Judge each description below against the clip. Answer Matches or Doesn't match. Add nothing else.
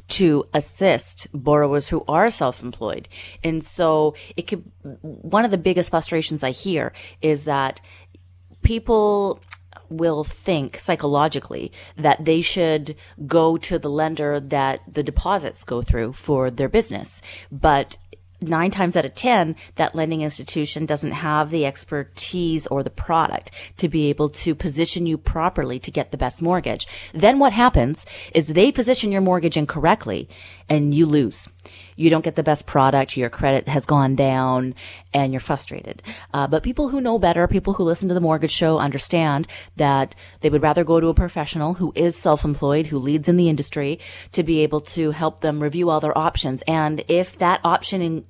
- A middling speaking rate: Matches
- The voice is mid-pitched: Matches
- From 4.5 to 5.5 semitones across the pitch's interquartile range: Doesn't match